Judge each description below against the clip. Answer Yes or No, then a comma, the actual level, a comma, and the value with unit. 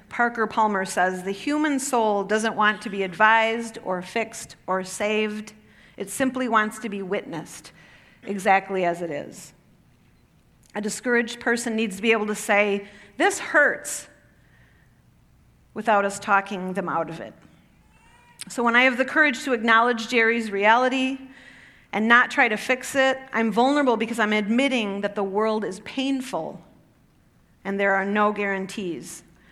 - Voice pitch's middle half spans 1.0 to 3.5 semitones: Yes, average, 3.2 semitones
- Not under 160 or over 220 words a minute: No, average, 150 wpm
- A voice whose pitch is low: No, high, 215 Hz